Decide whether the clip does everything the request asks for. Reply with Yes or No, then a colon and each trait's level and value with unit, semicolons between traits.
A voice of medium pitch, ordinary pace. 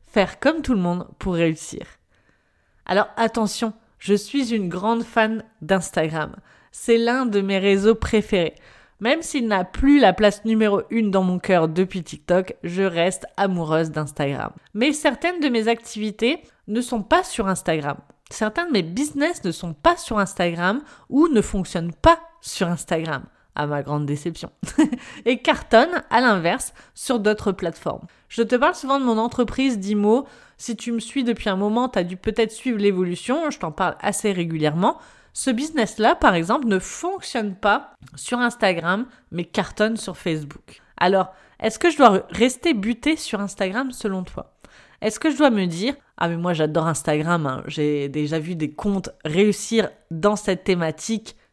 No: high, 210 Hz; average, 170 wpm